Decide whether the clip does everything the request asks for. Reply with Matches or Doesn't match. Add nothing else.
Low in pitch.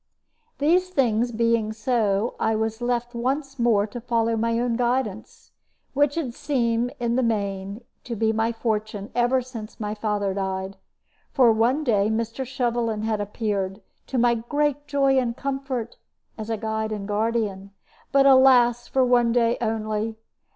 Doesn't match